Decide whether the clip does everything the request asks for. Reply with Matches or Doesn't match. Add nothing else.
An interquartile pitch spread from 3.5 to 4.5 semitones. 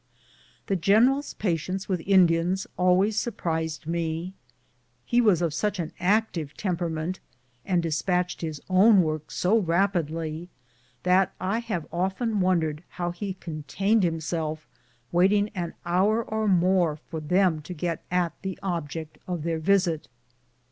Doesn't match